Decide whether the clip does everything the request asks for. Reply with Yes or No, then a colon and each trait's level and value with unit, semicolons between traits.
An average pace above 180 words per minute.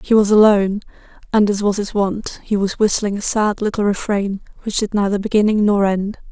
Yes: average, 200 wpm